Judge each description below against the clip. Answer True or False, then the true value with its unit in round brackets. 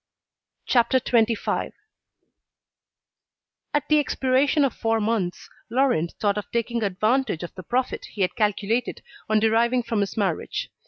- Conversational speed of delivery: False (130 wpm)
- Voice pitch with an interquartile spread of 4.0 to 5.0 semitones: False (3.6 semitones)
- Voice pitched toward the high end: True (225 Hz)